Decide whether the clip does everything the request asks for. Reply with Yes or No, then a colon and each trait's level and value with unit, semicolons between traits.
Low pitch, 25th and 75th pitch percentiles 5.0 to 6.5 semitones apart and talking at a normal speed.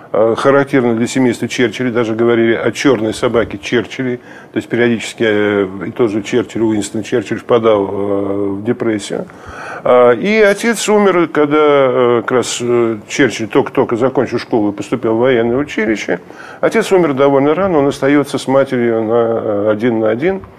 No: low, 120 Hz; average, 3.7 semitones; average, 145 wpm